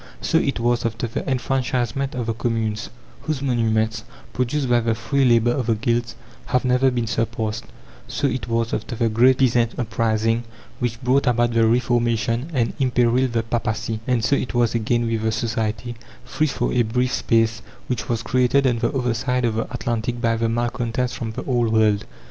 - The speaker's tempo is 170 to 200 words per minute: Yes, average, 190 wpm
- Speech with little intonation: Yes, narrow, 1.8 semitones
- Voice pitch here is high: No, low, 120 Hz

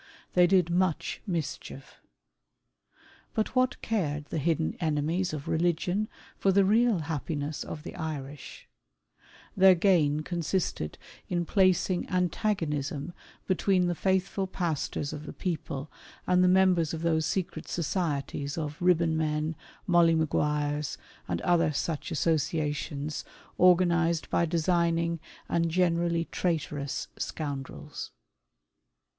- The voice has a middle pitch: Yes, medium, 165 Hz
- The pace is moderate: No, slow, 115 wpm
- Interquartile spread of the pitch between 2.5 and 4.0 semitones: Yes, average, 3.2 semitones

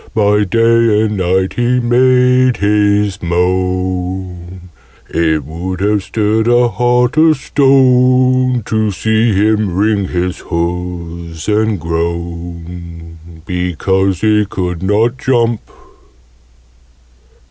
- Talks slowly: Yes, slow, 100 wpm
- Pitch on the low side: Yes, low, 100 Hz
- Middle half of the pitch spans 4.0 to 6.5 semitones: Yes, average, 4.6 semitones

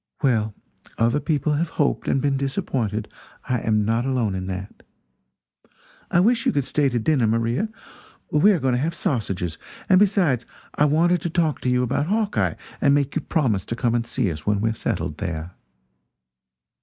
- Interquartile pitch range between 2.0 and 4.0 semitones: No, wide, 5.5 semitones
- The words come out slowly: No, average, 185 wpm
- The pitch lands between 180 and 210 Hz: No, low, 130 Hz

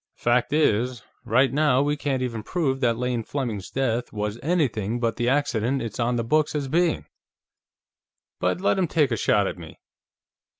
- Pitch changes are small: No, average, 4.0 semitones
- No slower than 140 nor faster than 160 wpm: No, average, 175 wpm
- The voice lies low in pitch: Yes, low, 125 Hz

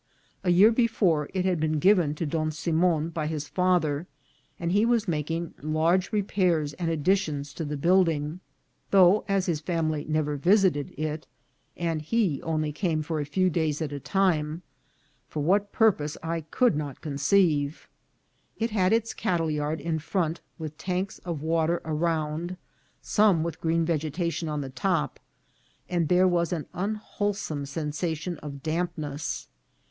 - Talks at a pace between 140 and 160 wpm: Yes, average, 150 wpm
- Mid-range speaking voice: Yes, medium, 165 Hz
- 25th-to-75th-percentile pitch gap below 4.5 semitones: Yes, average, 3.2 semitones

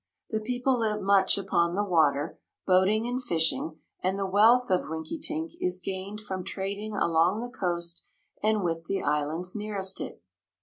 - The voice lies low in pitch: No, high, 190 Hz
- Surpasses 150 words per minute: Yes, average, 160 wpm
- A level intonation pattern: No, average, 3.8 semitones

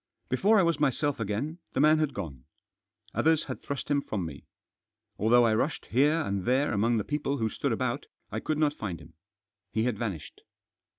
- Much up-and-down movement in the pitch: Yes, wide, 5.9 semitones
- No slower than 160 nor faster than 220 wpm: Yes, average, 190 wpm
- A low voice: Yes, low, 130 Hz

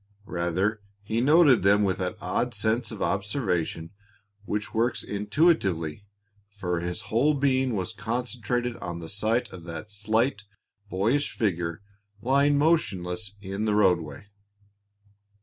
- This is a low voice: Yes, low, 105 Hz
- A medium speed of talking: No, slow, 125 wpm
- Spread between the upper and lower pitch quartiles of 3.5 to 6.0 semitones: Yes, average, 4.9 semitones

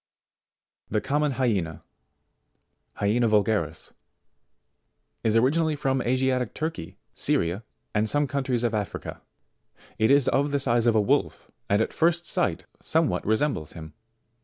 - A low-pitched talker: Yes, low, 120 Hz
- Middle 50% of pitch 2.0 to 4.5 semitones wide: No, average, 5.0 semitones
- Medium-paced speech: No, slow, 130 wpm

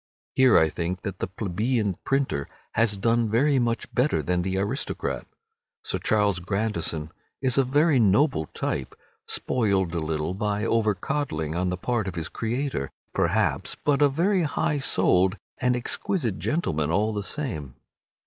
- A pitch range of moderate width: No, wide, 6.3 semitones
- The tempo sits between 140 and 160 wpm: Yes, average, 150 wpm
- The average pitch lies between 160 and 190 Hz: No, low, 105 Hz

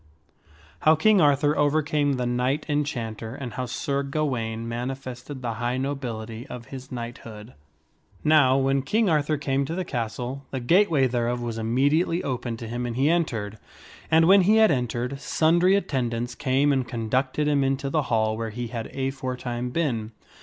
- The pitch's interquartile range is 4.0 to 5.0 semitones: No, average, 3.5 semitones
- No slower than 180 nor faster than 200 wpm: No, average, 165 wpm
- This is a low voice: Yes, low, 130 Hz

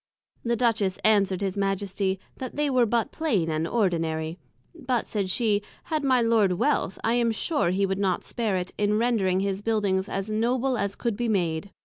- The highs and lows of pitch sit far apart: No, average, 3.7 semitones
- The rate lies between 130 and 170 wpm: No, average, 190 wpm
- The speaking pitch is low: No, high, 205 Hz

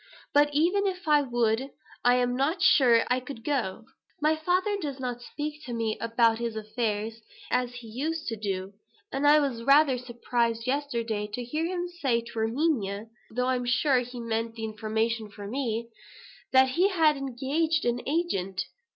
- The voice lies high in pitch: Yes, high, 245 Hz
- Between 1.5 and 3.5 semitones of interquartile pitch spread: No, average, 4.4 semitones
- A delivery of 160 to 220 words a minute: Yes, average, 175 wpm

